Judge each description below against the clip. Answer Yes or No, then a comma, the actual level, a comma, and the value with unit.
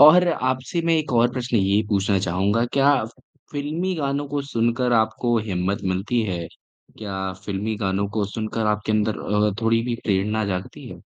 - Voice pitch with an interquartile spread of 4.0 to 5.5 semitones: Yes, average, 4.3 semitones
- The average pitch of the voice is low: Yes, low, 110 Hz